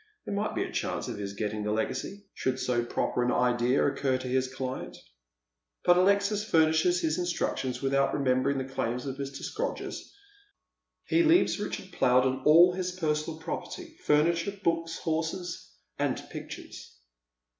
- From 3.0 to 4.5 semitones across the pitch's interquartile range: No, wide, 5.5 semitones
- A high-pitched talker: No, medium, 150 Hz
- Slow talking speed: No, average, 155 wpm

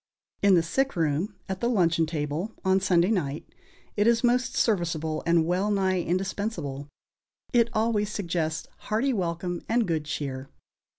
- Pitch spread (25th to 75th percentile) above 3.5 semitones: Yes, average, 4.5 semitones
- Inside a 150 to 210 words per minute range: No, average, 140 wpm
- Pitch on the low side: No, medium, 185 Hz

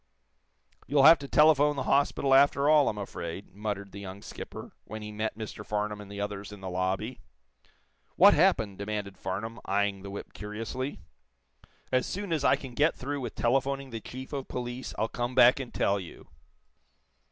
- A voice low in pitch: Yes, low, 110 Hz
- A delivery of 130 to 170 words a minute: No, average, 180 wpm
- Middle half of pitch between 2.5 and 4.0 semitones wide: No, average, 4.9 semitones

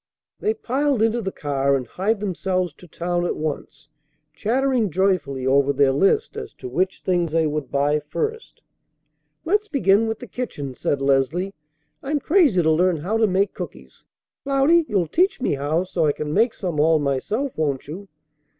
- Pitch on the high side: No, medium, 180 Hz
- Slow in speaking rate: No, average, 175 wpm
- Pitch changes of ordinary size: No, wide, 7.8 semitones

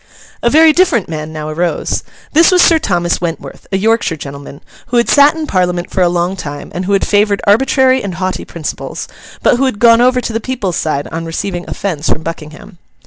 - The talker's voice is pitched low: No, high, 195 Hz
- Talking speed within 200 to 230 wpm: Yes, fast, 205 wpm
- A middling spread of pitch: No, wide, 6.5 semitones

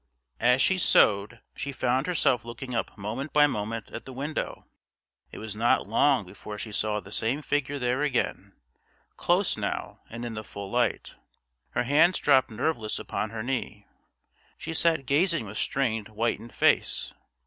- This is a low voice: Yes, low, 120 Hz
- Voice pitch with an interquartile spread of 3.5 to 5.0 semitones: Yes, average, 4.5 semitones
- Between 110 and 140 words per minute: No, average, 160 wpm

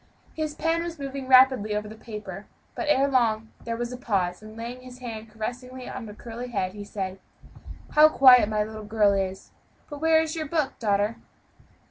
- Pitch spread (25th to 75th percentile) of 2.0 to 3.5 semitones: No, average, 4.0 semitones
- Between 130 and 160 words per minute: No, average, 190 wpm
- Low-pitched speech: No, high, 235 Hz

